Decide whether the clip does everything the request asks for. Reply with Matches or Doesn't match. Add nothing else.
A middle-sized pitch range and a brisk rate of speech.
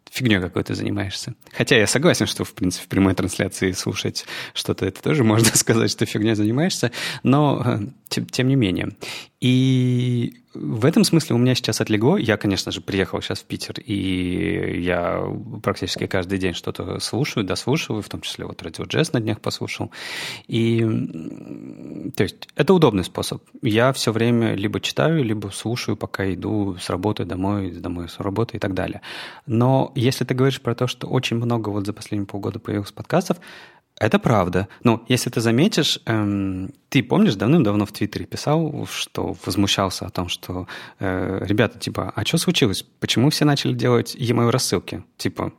Matches